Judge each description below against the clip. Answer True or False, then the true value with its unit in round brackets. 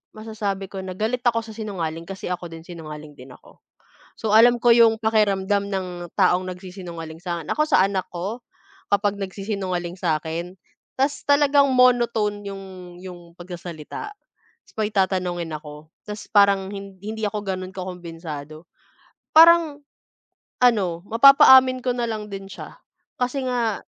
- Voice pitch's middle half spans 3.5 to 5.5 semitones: True (4.3 semitones)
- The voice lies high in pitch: True (195 Hz)